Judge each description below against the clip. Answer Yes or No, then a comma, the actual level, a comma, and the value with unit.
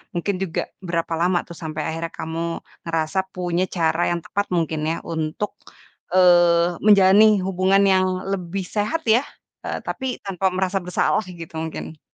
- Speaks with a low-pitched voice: No, medium, 175 Hz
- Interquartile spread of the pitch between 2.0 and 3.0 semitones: Yes, narrow, 2.6 semitones